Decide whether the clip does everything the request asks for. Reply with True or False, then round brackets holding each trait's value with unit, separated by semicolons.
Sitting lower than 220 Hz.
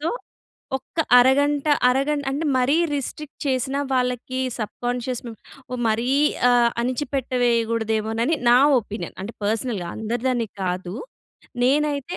False (250 Hz)